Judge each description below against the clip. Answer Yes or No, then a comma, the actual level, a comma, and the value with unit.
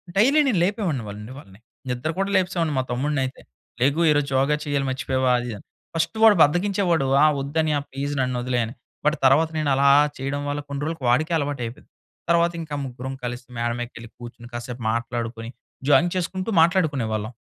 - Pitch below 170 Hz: Yes, medium, 140 Hz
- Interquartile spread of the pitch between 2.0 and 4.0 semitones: No, average, 5.0 semitones